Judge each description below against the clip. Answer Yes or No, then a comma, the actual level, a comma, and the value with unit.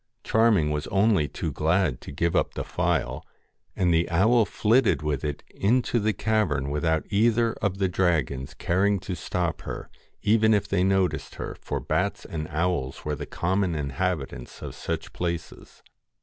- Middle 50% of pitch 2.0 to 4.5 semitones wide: No, average, 5.1 semitones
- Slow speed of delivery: No, average, 165 wpm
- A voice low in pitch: Yes, very low, 90 Hz